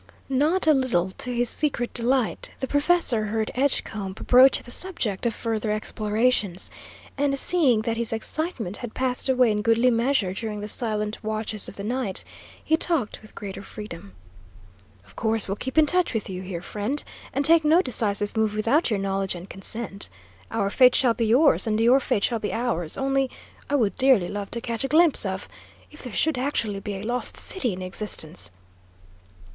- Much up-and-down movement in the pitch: No, average, 4.2 semitones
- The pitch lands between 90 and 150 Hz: No, high, 230 Hz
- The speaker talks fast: No, average, 185 wpm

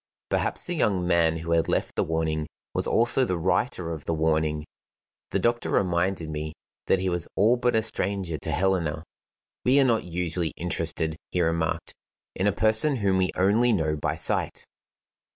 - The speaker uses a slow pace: No, average, 175 wpm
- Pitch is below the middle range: Yes, very low, 90 Hz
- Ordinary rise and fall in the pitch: Yes, average, 4.1 semitones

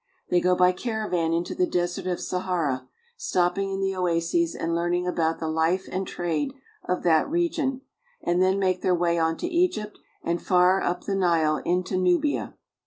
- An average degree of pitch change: No, narrow, 2.2 semitones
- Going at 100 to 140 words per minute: No, average, 175 wpm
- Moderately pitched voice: Yes, medium, 180 Hz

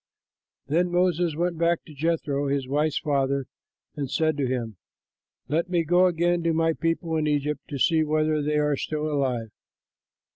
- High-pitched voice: No, medium, 155 Hz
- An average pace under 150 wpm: No, average, 170 wpm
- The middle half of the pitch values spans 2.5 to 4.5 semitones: Yes, average, 2.8 semitones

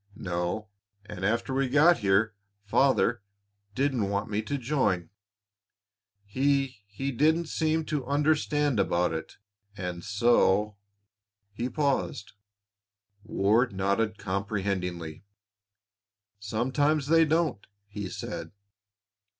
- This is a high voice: No, low, 110 Hz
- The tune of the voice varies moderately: No, wide, 5.9 semitones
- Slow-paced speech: Yes, slow, 100 wpm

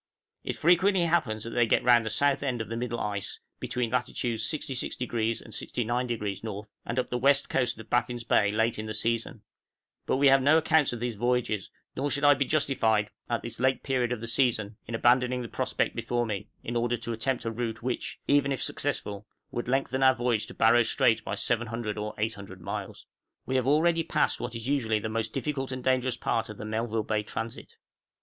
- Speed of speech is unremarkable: No, fast, 210 wpm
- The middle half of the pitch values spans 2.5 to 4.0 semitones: Yes, average, 2.9 semitones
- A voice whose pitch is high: No, low, 120 Hz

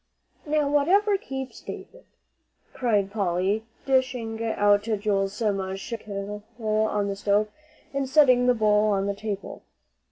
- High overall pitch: Yes, high, 215 Hz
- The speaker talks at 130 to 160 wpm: Yes, slow, 135 wpm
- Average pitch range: Yes, average, 4.2 semitones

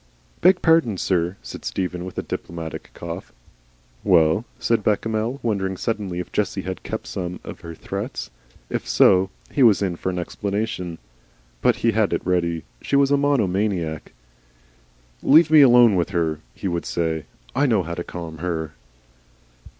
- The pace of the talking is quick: No, average, 160 wpm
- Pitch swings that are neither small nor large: Yes, average, 4.7 semitones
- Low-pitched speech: Yes, very low, 95 Hz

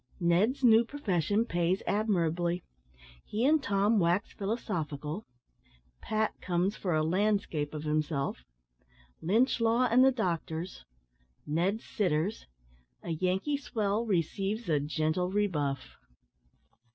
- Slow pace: Yes, slow, 110 wpm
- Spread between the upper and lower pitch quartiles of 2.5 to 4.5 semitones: No, average, 5.1 semitones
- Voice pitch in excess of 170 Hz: Yes, high, 190 Hz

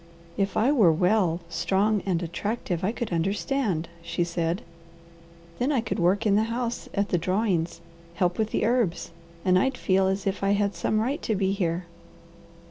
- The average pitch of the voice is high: Yes, high, 195 Hz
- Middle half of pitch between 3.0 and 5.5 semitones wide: Yes, average, 3.9 semitones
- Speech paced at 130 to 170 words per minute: No, average, 180 wpm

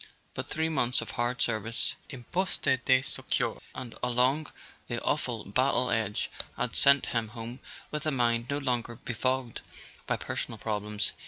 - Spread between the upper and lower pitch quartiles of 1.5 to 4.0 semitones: Yes, narrow, 2.4 semitones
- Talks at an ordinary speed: Yes, average, 160 wpm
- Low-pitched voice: Yes, low, 125 Hz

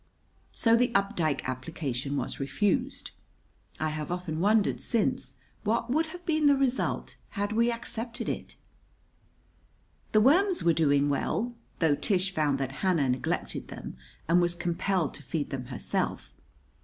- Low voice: No, medium, 180 Hz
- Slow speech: No, average, 145 wpm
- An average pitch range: No, wide, 8.1 semitones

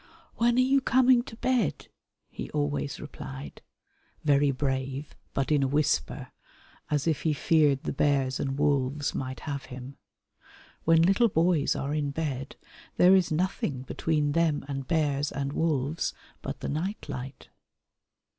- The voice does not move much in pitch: No, average, 3.5 semitones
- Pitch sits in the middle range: Yes, medium, 145 Hz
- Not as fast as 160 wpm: Yes, average, 145 wpm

